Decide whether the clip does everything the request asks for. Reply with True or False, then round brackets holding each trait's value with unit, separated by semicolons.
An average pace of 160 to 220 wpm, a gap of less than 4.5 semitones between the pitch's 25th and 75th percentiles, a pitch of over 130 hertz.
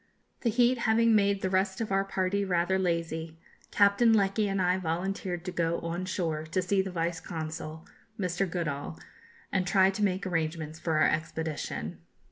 True (170 wpm; 3.1 semitones; 185 Hz)